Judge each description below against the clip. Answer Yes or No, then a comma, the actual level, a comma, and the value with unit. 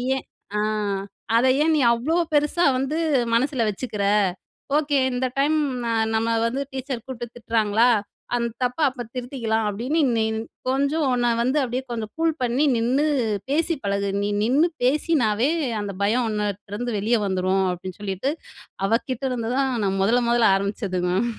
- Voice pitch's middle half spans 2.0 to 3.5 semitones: No, average, 4.2 semitones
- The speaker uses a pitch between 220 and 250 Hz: Yes, high, 240 Hz